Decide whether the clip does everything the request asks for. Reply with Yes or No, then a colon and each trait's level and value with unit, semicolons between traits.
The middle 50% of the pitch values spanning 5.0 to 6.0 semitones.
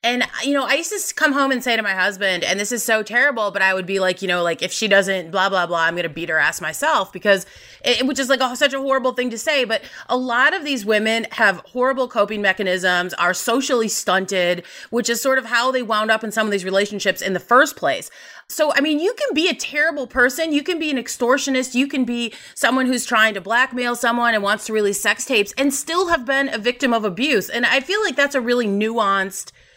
Yes: average, 5.3 semitones